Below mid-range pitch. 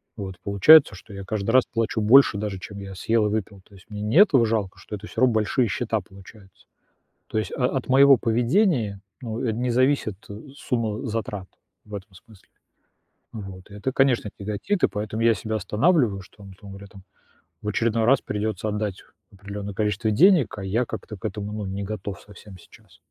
Yes: low, 105 Hz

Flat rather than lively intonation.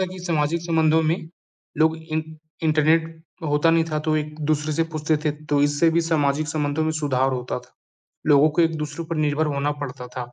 Yes: narrow, 1.6 semitones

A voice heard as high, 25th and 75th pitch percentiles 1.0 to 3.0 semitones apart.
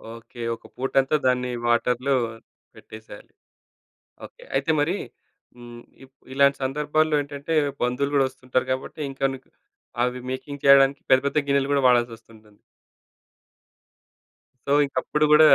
No: low, 135 Hz; narrow, 2.4 semitones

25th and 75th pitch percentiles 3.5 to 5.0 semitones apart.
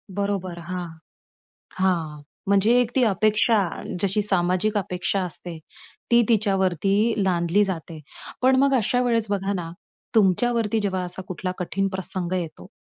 No: average, 3.1 semitones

